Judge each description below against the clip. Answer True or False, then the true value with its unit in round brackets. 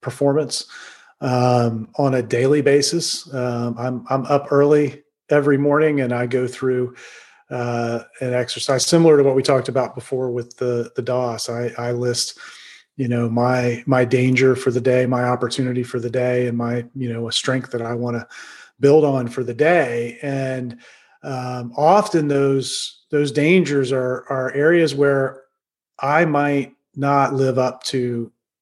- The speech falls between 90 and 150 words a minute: False (165 wpm)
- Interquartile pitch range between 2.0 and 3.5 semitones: True (2.4 semitones)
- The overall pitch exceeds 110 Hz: True (130 Hz)